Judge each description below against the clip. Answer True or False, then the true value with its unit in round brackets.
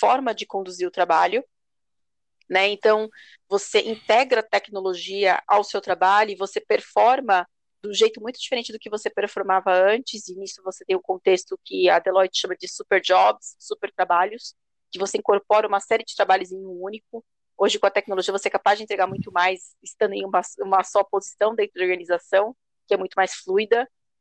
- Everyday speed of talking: False (195 wpm)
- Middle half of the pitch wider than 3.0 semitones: False (2.7 semitones)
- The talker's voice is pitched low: False (200 Hz)